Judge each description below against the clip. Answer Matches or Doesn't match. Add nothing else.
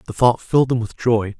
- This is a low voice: Matches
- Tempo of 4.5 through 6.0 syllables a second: Matches